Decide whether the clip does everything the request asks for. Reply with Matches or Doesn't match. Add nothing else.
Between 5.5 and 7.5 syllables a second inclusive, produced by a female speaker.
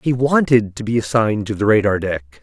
Doesn't match